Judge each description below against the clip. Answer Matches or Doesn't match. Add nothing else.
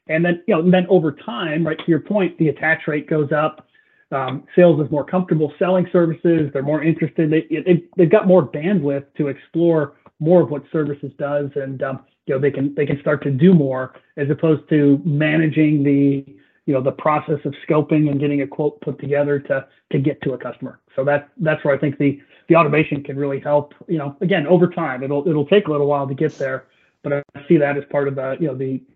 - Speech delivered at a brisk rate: Matches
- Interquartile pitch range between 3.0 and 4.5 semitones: Doesn't match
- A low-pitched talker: Doesn't match